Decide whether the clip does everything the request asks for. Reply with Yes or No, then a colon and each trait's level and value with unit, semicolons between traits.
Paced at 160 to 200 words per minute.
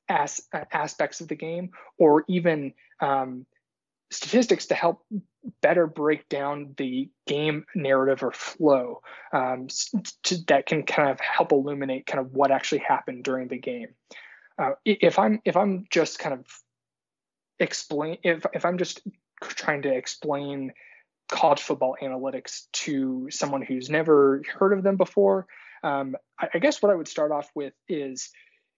No: average, 150 wpm